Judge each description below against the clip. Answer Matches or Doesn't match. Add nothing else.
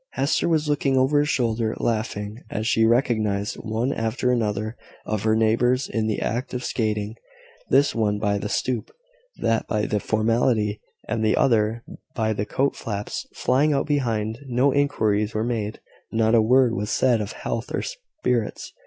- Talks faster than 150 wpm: Matches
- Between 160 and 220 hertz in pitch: Doesn't match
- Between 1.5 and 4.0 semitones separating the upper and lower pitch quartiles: Matches